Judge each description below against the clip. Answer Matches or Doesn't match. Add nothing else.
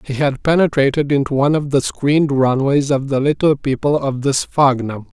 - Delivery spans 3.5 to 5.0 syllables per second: Doesn't match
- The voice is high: Doesn't match